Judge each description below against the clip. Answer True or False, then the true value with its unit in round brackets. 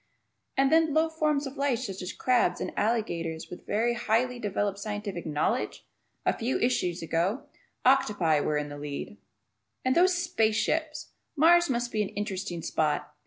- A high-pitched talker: True (220 Hz)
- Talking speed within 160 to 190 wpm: True (165 wpm)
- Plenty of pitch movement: True (7.2 semitones)